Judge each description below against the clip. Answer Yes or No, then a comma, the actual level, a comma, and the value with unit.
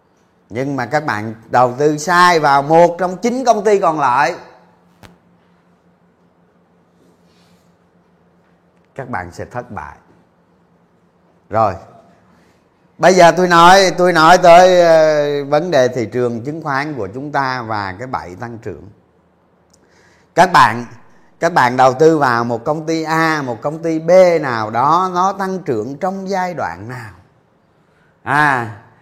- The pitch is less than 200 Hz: Yes, low, 135 Hz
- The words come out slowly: Yes, slow, 140 wpm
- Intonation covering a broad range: Yes, wide, 7.5 semitones